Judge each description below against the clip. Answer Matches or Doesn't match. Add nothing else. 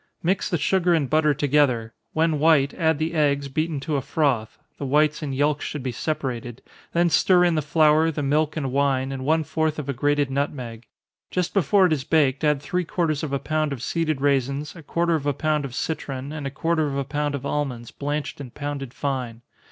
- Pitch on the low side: Doesn't match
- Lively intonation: Doesn't match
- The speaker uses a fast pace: Matches